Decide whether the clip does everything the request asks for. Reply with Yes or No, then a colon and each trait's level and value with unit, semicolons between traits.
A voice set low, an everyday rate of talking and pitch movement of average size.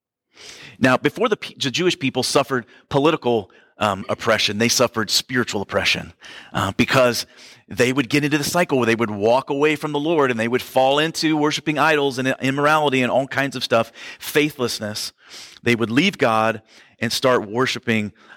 Yes: low, 125 Hz; average, 175 wpm; average, 3.9 semitones